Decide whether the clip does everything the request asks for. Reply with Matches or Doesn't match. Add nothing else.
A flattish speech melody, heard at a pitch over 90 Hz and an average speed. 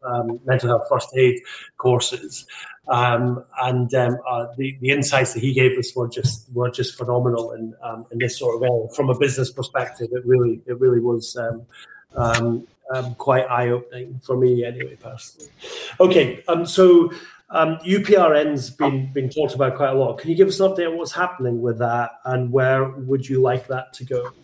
Matches